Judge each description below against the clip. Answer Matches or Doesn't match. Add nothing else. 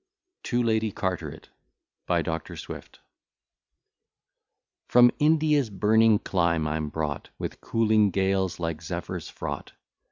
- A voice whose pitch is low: Matches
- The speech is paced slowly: Matches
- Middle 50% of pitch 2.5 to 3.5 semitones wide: Doesn't match